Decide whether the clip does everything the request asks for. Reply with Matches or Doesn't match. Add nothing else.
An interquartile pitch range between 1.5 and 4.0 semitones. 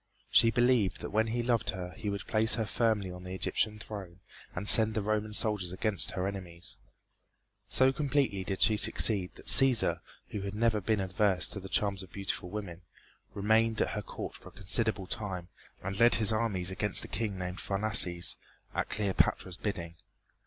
Matches